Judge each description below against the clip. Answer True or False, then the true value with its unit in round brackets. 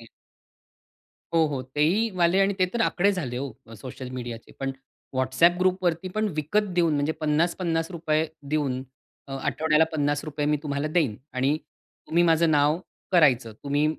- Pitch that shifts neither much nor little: True (3.5 semitones)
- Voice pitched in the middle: True (155 Hz)